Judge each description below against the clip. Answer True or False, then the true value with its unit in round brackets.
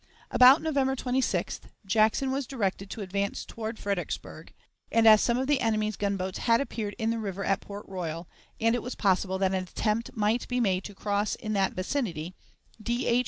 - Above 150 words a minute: True (190 wpm)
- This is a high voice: True (215 Hz)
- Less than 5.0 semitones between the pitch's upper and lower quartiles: True (3.5 semitones)